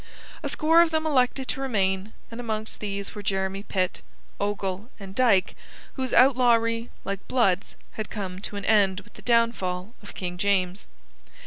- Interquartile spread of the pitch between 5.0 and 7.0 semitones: No, average, 3.9 semitones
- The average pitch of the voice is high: Yes, high, 205 Hz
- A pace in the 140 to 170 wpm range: Yes, average, 160 wpm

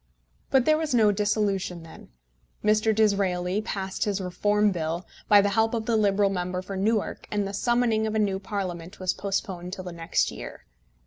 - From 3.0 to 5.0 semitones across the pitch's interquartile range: No, narrow, 2.6 semitones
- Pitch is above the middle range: Yes, high, 200 Hz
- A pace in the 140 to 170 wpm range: No, average, 185 wpm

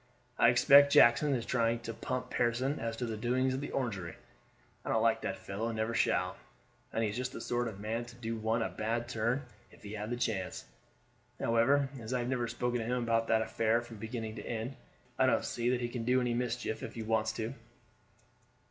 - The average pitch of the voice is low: Yes, low, 115 Hz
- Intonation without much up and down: Yes, narrow, 1.8 semitones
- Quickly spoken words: Yes, fast, 225 wpm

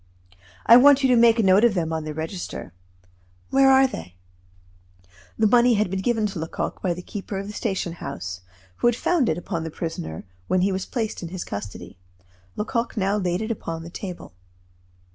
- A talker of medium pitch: No, high, 195 Hz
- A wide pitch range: Yes, wide, 5.8 semitones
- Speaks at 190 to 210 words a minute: Yes, average, 200 wpm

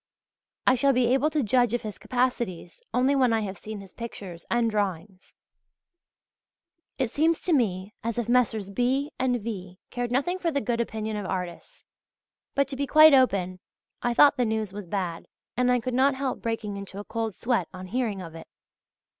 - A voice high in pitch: Yes, high, 230 Hz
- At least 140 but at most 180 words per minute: No, average, 190 wpm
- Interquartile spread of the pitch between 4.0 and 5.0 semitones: Yes, average, 4.5 semitones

